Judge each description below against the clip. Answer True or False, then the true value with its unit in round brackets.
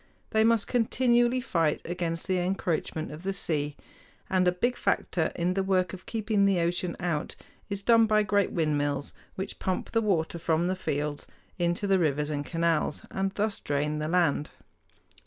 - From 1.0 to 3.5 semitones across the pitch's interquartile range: False (4.1 semitones)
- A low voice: False (180 Hz)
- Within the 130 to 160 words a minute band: False (175 wpm)